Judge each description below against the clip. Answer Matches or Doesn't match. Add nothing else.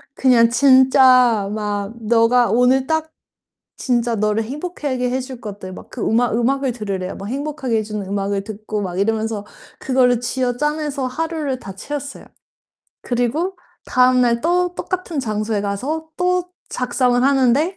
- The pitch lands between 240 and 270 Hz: Matches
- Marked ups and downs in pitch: Doesn't match